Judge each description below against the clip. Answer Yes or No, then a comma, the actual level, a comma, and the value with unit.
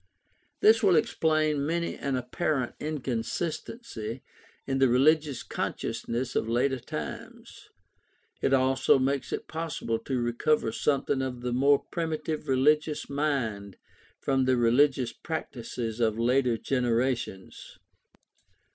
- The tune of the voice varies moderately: Yes, average, 3.9 semitones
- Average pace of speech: No, slow, 110 wpm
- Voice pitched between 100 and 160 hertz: Yes, low, 135 Hz